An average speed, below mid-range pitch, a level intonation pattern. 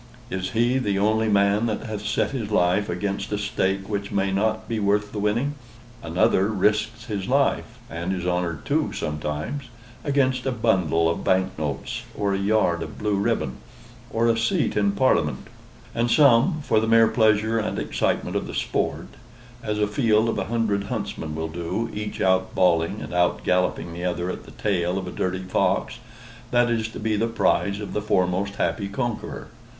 No: average, 185 wpm; low, 105 Hz; average, 3.3 semitones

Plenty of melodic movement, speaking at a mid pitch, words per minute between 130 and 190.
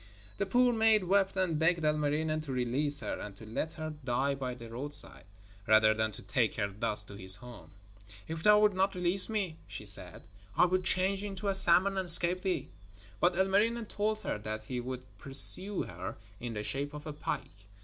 No: wide, 7.9 semitones; medium, 155 Hz; average, 200 wpm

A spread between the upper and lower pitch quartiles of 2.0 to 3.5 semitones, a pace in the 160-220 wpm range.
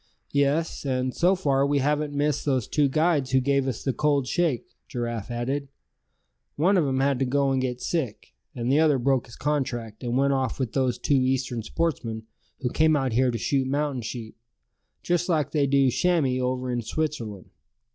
Yes: average, 2.7 semitones; average, 190 wpm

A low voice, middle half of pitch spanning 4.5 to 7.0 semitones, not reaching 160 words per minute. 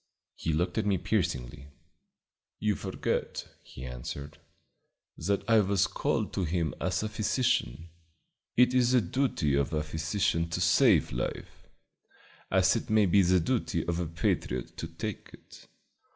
Yes: very low, 85 Hz; average, 5.1 semitones; average, 150 wpm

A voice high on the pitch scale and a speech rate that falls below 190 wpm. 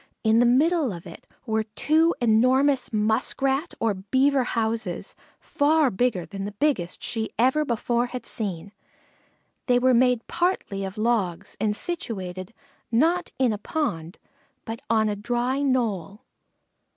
Yes: high, 235 Hz; average, 140 wpm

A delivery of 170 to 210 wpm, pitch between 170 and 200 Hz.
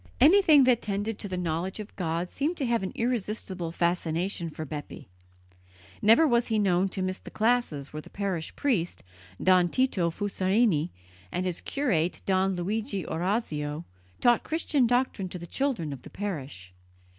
No: average, 160 wpm; high, 190 Hz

